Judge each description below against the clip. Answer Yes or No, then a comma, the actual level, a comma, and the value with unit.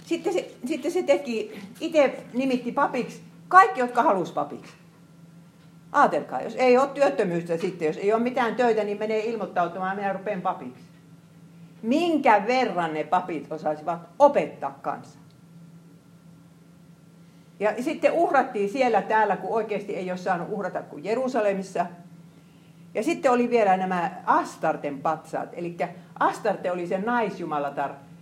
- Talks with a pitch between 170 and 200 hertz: Yes, medium, 185 Hz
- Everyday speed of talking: Yes, average, 130 wpm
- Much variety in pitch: Yes, wide, 6.0 semitones